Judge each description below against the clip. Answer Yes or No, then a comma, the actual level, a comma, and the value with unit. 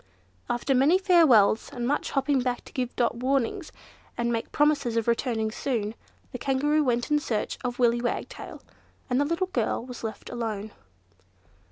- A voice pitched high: Yes, very high, 250 Hz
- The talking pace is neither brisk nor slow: Yes, average, 170 wpm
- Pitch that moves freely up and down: No, average, 3.5 semitones